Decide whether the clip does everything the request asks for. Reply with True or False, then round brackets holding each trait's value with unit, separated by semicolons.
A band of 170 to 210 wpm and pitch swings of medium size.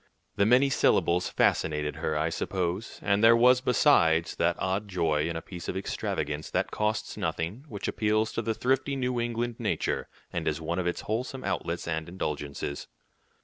False (175 wpm; 6.1 semitones)